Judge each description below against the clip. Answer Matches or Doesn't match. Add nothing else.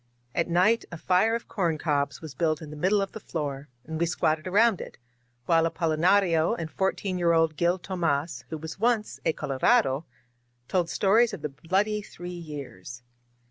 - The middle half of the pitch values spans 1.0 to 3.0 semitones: Doesn't match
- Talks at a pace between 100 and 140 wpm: Doesn't match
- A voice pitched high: Doesn't match